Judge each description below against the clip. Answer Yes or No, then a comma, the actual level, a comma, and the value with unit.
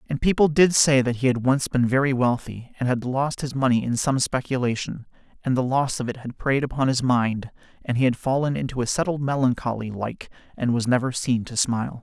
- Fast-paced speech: Yes, fast, 220 wpm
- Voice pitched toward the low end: Yes, low, 130 Hz